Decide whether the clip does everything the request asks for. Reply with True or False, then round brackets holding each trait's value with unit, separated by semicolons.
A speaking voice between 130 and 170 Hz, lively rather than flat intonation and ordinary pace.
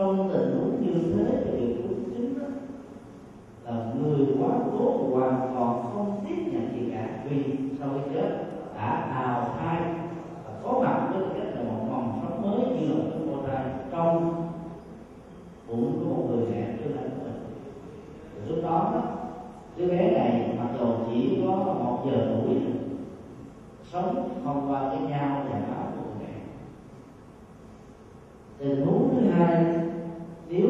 False (140 Hz; 6.0 semitones; 145 wpm)